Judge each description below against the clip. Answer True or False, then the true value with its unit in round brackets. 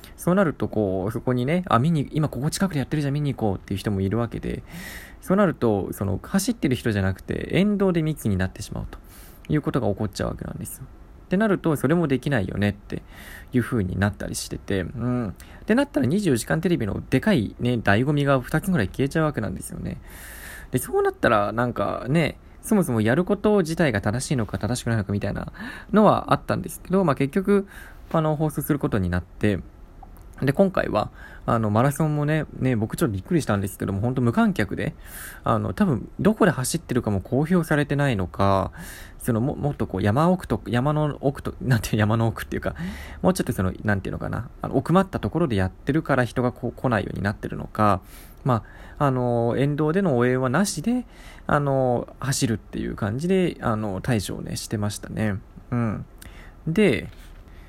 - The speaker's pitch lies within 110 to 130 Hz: True (120 Hz)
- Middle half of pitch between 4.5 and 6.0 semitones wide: False (7.3 semitones)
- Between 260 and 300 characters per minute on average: False (410 characters per minute)